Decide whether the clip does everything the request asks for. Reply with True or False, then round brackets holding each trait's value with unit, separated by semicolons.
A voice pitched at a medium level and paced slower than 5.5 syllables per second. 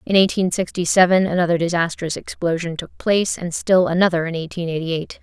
False (175 Hz; 5.9 syllables/s)